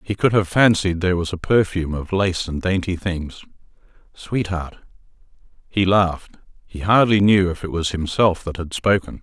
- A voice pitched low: Yes, very low, 95 Hz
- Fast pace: No, average, 165 wpm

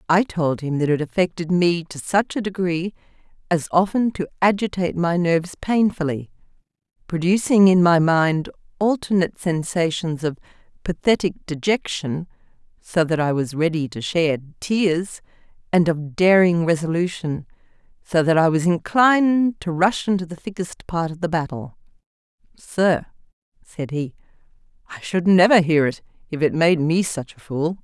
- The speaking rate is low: No, average, 145 wpm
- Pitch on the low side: No, medium, 170 Hz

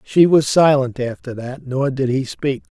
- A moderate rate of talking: Yes, average, 195 wpm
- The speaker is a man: Yes, male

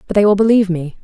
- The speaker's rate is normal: No, fast, 290 wpm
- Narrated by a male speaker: No, female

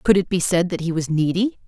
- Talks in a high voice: No, medium, 175 Hz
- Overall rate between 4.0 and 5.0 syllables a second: No, 6.0 syllables/s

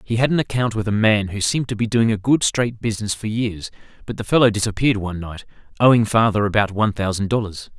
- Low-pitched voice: Yes, low, 110 Hz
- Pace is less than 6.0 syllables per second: No, 6.5 syllables/s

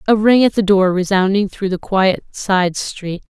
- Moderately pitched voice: No, high, 195 Hz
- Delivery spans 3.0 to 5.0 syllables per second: Yes, 4.3 syllables/s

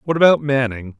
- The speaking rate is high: No, average, 180 wpm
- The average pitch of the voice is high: No, low, 130 Hz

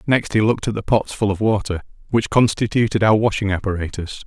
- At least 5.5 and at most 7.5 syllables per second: Yes, 6.0 syllables/s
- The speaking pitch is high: No, low, 105 Hz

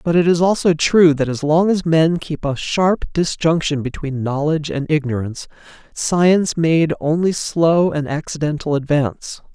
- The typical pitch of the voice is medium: Yes, medium, 155 Hz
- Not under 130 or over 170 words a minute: Yes, average, 155 wpm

